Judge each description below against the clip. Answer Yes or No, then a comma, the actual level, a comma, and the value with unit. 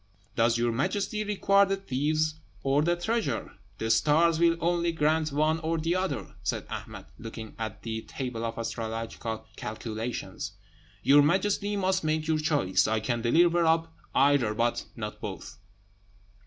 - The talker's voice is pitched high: No, medium, 150 Hz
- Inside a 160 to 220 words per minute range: No, average, 150 wpm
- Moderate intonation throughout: No, wide, 6.6 semitones